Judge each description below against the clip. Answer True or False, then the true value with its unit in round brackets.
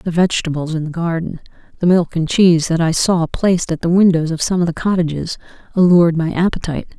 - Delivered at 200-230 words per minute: True (205 wpm)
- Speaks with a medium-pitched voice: True (170 Hz)